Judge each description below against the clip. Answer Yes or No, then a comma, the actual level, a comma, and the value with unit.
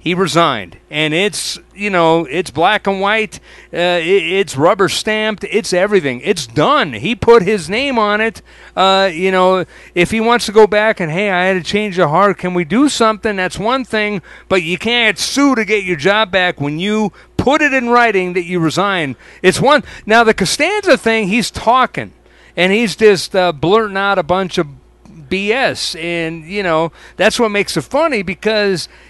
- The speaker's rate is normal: Yes, average, 190 wpm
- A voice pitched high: Yes, high, 195 Hz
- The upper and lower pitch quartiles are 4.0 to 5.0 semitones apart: No, average, 3.6 semitones